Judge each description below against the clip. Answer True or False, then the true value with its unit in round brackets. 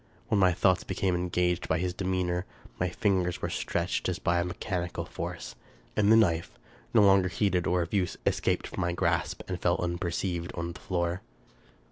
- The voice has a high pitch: False (90 Hz)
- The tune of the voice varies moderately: False (1.4 semitones)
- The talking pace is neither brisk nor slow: True (180 wpm)